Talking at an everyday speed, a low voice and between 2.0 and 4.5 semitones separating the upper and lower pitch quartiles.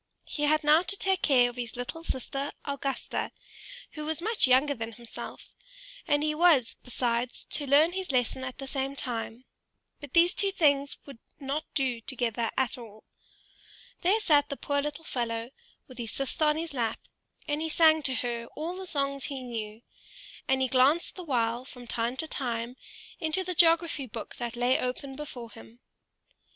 No: average, 180 wpm; very high, 270 Hz; average, 4.1 semitones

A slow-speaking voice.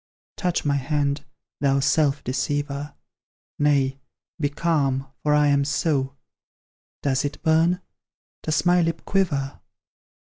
Yes: slow, 115 wpm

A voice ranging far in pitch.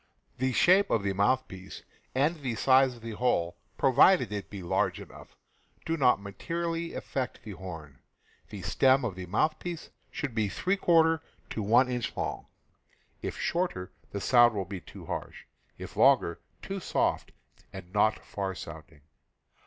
Yes: wide, 7.7 semitones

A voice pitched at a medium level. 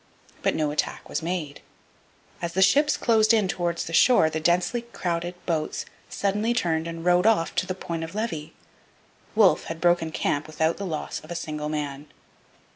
Yes: medium, 170 Hz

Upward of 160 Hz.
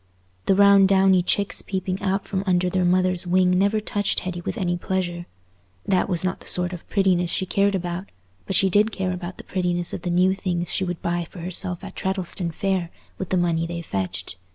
Yes: medium, 185 Hz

